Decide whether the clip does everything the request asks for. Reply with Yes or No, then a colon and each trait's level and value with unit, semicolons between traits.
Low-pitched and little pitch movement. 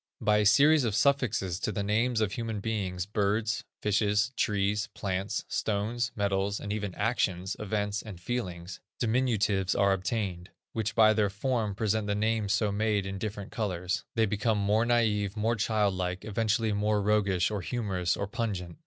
Yes: low, 105 Hz; narrow, 2.2 semitones